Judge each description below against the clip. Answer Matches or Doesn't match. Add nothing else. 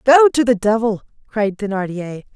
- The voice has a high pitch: Matches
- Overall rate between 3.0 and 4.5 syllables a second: Doesn't match